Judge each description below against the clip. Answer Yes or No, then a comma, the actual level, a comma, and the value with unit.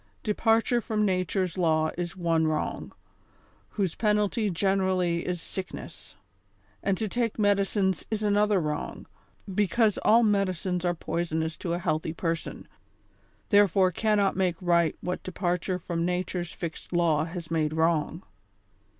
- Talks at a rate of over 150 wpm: No, slow, 135 wpm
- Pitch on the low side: No, medium, 180 Hz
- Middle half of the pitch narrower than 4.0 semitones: Yes, average, 3.3 semitones